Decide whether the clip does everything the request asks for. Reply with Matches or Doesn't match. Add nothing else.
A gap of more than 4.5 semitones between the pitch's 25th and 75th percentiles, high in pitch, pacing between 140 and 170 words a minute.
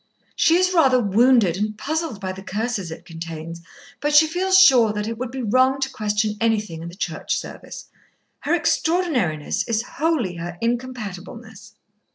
Matches